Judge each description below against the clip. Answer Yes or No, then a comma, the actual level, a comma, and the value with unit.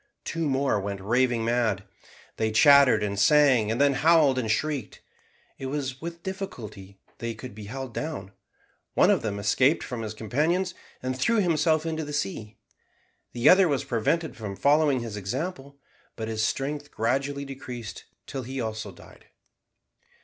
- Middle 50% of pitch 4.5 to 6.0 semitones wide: Yes, average, 5.1 semitones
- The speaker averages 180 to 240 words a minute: No, average, 155 wpm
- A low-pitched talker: Yes, low, 130 Hz